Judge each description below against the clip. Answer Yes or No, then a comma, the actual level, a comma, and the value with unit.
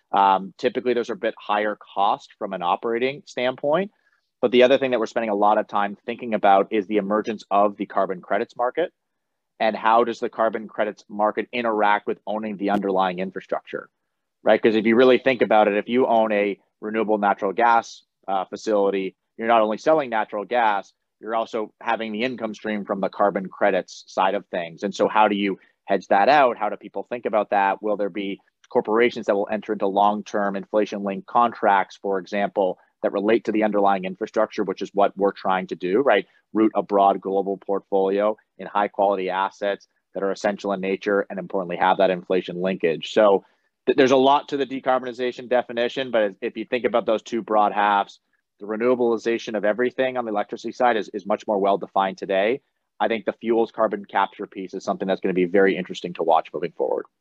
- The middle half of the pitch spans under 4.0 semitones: Yes, average, 2.9 semitones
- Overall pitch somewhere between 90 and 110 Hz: Yes, low, 105 Hz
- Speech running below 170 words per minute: No, fast, 205 wpm